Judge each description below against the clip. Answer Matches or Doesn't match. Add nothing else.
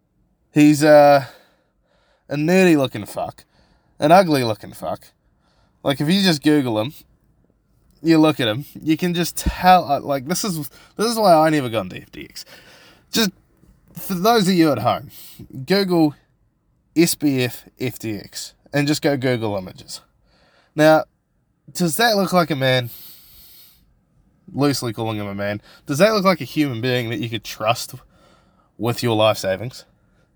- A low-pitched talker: Doesn't match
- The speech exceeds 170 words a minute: Doesn't match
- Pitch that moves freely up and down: Matches